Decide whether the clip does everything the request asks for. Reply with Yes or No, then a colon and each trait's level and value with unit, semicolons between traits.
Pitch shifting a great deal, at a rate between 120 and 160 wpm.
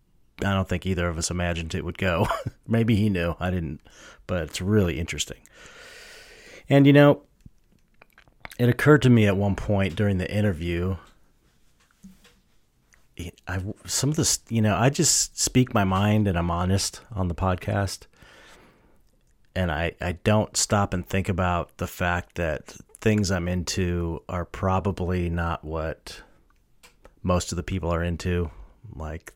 No: average, 3.5 semitones; average, 150 wpm